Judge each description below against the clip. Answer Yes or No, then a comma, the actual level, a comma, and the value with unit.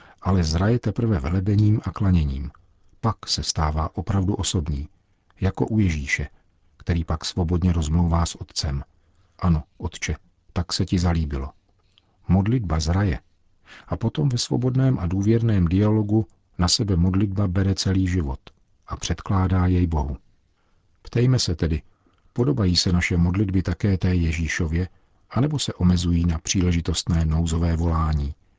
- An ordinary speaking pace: Yes, average, 130 wpm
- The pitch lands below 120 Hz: Yes, very low, 90 Hz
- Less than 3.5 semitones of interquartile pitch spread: Yes, average, 2.7 semitones